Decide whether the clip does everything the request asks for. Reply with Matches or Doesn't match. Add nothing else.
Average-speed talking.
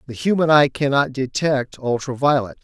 Matches